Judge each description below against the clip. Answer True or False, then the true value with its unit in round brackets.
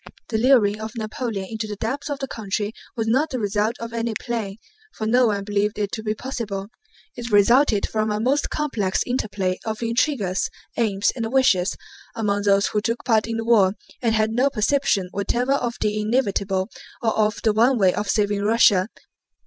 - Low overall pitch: False (220 Hz)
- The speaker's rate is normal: True (190 wpm)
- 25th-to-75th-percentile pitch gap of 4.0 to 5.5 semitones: False (2.6 semitones)